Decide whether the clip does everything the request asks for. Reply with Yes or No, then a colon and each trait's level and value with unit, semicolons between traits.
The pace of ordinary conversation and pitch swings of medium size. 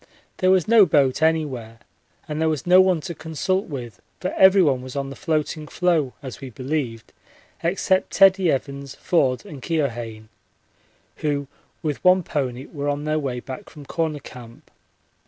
Yes: average, 160 wpm; average, 4.3 semitones